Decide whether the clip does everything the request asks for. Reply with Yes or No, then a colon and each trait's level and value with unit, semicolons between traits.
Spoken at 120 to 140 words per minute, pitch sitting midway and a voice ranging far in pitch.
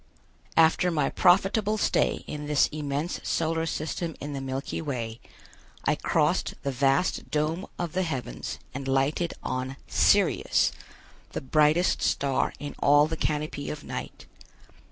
No: slow, 135 wpm; medium, 150 Hz; average, 3.1 semitones